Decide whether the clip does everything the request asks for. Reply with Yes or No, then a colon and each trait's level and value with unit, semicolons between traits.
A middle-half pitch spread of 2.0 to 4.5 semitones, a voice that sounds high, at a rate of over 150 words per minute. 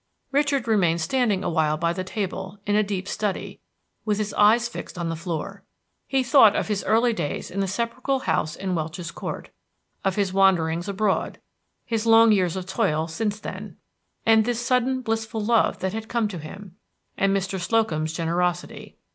Yes: average, 4.0 semitones; high, 200 Hz; average, 175 wpm